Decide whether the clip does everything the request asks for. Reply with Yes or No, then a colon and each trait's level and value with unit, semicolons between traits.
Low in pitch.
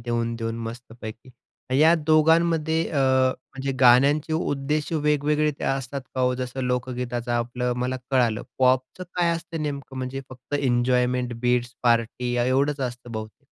Yes: low, 130 Hz